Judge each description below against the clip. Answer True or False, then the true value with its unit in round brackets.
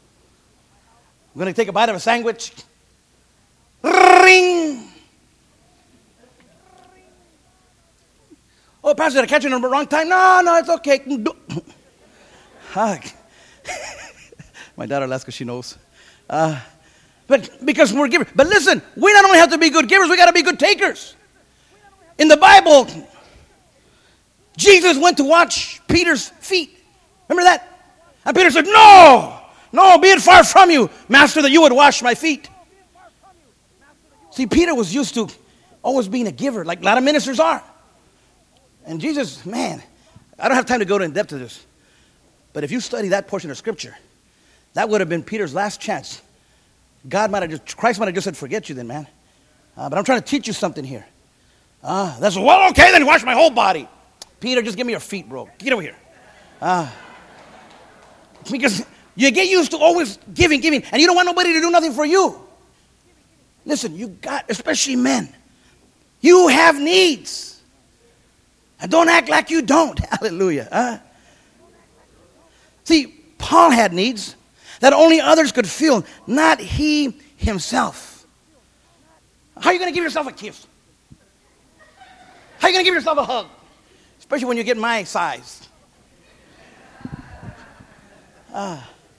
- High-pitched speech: True (280 Hz)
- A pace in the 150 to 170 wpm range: True (155 wpm)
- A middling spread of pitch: False (7.8 semitones)